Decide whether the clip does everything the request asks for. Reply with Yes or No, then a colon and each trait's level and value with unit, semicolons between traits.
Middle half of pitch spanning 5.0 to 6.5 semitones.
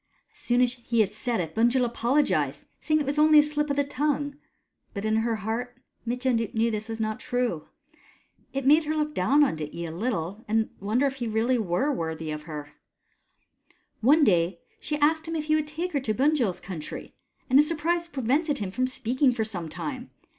Yes: wide, 5.4 semitones